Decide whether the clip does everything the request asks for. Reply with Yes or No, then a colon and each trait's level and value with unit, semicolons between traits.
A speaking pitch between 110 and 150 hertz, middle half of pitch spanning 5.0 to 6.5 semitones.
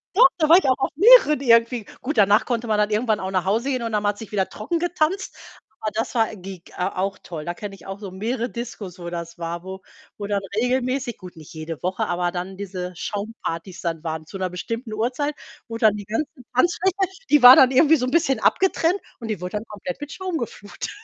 No: high, 215 Hz; wide, 5.6 semitones